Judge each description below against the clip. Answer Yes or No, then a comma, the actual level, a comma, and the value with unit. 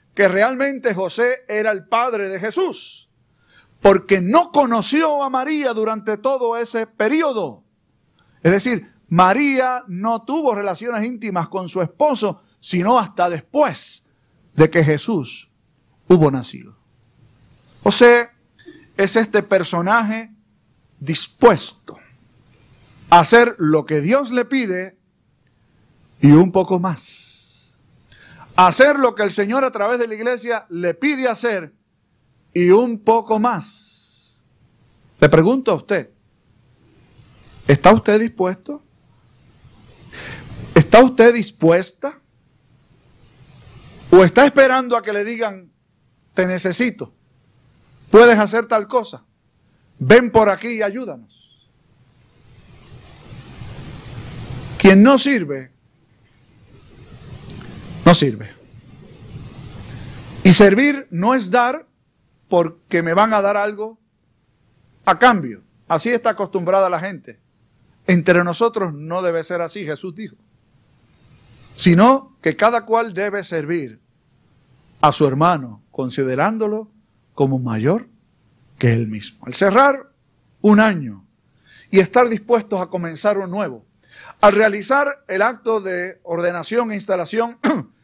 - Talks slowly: Yes, slow, 110 wpm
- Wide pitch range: Yes, wide, 8.8 semitones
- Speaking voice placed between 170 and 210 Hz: Yes, medium, 185 Hz